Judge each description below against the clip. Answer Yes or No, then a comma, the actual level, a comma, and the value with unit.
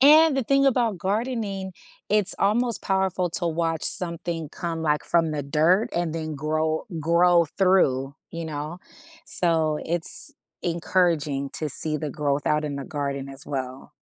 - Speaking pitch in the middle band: Yes, medium, 165 Hz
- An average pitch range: Yes, average, 3.9 semitones